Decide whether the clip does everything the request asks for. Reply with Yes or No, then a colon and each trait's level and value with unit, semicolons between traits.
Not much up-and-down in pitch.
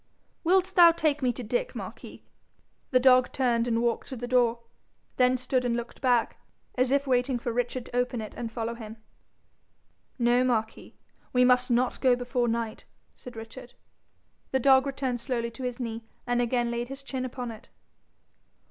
Yes: narrow, 1.6 semitones